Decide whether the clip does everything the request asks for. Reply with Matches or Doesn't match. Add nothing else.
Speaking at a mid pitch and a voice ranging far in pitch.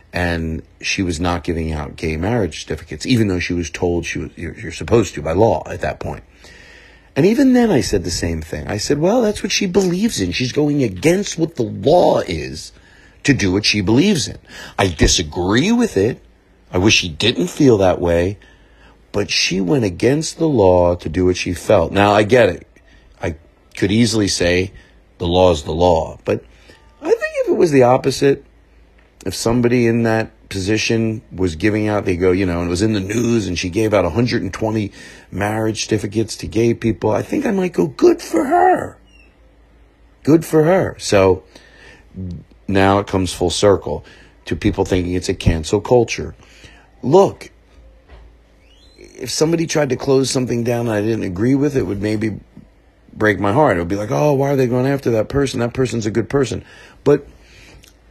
Doesn't match